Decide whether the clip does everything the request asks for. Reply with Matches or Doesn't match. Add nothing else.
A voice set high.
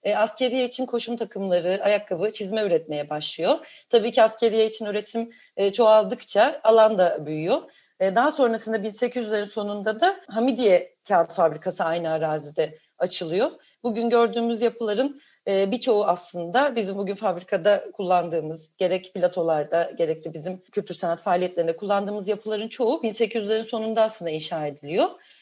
Matches